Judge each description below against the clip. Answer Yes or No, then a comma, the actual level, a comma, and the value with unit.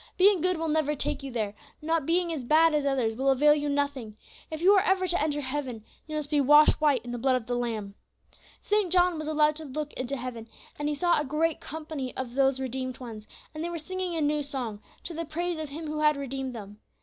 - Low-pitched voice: No, very high, 295 Hz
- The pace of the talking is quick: Yes, fast, 245 wpm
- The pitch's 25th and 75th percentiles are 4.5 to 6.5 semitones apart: No, average, 3.6 semitones